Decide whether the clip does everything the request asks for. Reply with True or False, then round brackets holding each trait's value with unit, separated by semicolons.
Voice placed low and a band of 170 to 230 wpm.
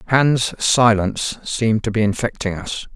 False (110 Hz; 140 wpm)